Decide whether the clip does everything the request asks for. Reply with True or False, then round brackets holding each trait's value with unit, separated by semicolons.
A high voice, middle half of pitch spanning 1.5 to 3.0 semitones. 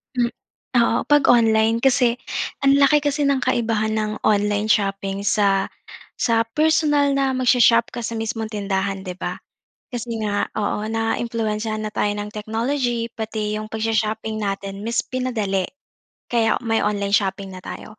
True (220 Hz; 2.4 semitones)